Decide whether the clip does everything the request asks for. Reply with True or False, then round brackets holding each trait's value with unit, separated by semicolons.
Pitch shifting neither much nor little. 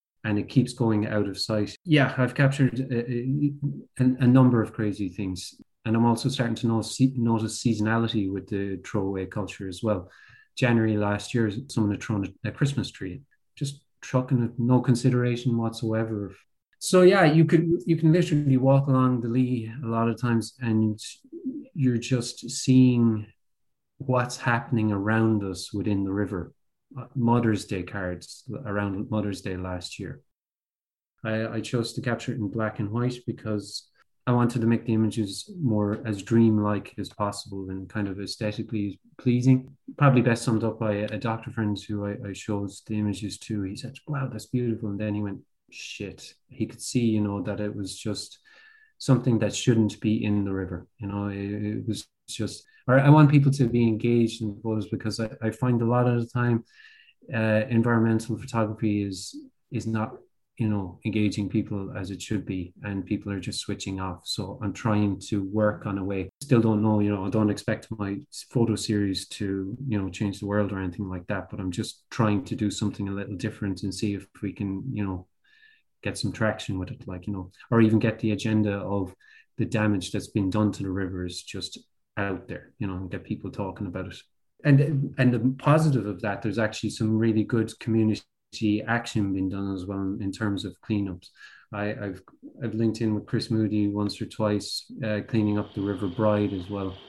True (3.1 semitones)